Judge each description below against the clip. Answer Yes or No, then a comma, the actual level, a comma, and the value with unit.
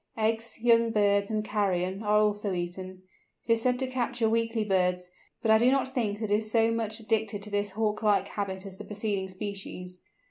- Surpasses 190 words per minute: Yes, average, 200 wpm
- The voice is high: Yes, high, 210 Hz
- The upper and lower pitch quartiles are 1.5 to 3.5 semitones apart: Yes, narrow, 2.4 semitones